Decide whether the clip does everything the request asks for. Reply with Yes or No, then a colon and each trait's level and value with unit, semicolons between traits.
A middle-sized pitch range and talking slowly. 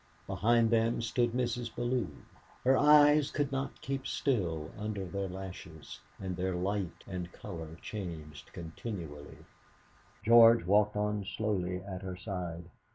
Yes: average, 4.8 semitones; slow, 130 wpm